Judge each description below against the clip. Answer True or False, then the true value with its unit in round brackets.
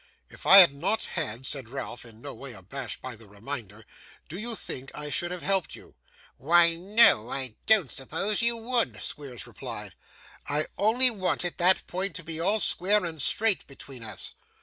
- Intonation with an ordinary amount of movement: False (7.1 semitones)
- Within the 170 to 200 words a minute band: True (180 wpm)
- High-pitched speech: False (165 Hz)